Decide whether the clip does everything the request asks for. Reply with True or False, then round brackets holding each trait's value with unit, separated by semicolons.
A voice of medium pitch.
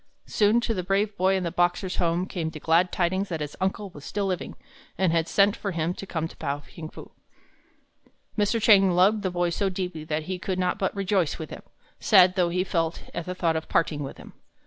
True (180 Hz)